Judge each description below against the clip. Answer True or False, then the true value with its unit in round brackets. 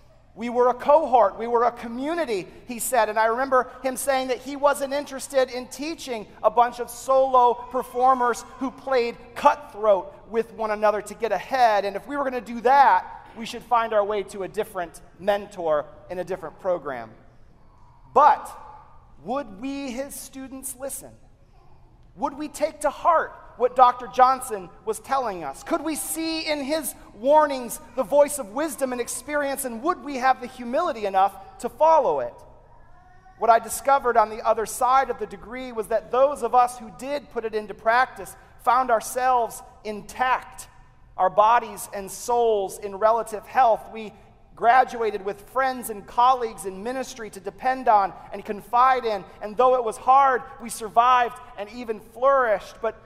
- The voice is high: True (245 Hz)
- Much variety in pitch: False (3.8 semitones)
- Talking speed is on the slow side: False (170 wpm)